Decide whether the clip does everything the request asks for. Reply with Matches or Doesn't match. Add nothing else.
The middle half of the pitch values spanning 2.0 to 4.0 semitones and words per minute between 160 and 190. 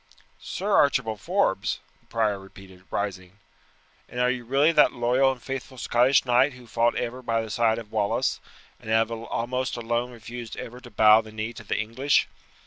Matches